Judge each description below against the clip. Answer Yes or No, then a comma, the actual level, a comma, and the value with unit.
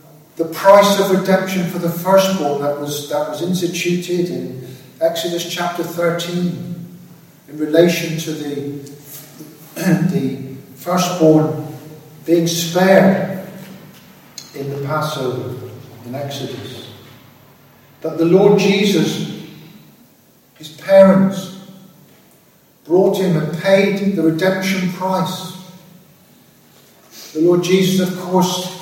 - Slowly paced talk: Yes, slow, 100 wpm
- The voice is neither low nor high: Yes, medium, 170 Hz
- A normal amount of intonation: Yes, average, 3.7 semitones